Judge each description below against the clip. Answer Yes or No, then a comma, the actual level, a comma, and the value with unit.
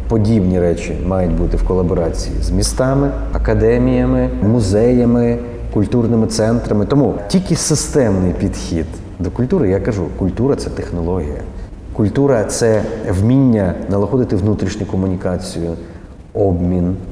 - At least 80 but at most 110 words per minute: Yes, slow, 105 wpm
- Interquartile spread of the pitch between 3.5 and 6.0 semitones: Yes, average, 4.7 semitones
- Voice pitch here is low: Yes, low, 100 Hz